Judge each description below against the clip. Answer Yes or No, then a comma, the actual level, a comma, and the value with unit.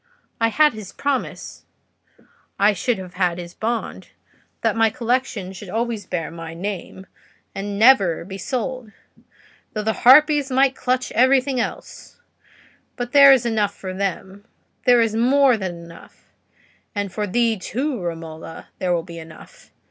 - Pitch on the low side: No, high, 215 Hz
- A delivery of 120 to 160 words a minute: Yes, average, 140 wpm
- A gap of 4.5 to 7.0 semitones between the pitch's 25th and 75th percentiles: Yes, average, 5.3 semitones